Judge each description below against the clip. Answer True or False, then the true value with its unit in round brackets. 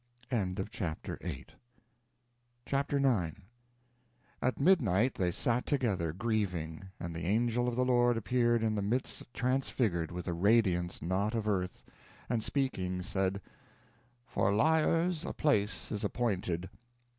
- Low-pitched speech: True (110 Hz)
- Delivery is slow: True (120 wpm)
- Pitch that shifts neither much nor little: True (4.9 semitones)